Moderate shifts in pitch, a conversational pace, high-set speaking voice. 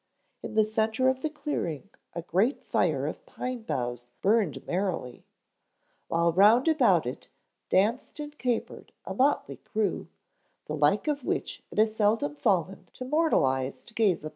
No: wide, 7.3 semitones; average, 160 wpm; high, 210 Hz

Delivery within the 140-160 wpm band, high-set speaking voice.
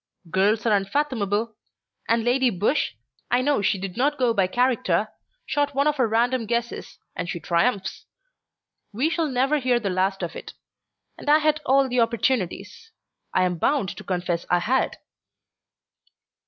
Yes: average, 155 wpm; high, 235 Hz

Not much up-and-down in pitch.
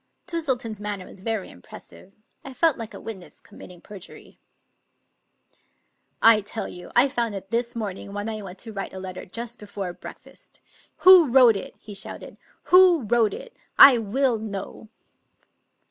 No: average, 3.6 semitones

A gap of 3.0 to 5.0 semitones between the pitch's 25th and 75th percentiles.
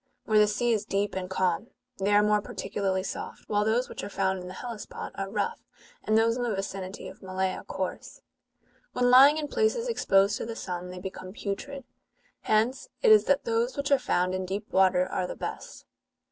Yes: average, 4.3 semitones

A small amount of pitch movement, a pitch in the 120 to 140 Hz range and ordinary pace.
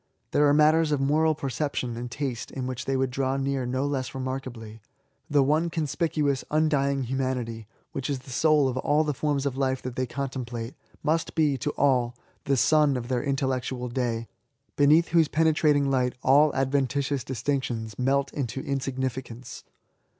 Yes: narrow, 2.3 semitones; low, 135 Hz; average, 180 wpm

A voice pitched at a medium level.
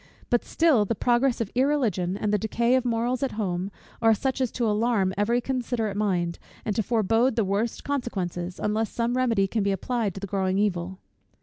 No: high, 220 Hz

